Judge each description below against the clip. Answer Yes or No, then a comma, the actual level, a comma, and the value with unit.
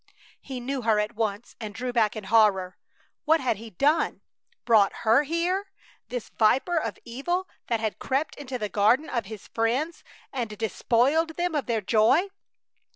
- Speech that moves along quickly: No, average, 165 wpm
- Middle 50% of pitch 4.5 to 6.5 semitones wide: Yes, average, 5.1 semitones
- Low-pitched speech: No, high, 235 Hz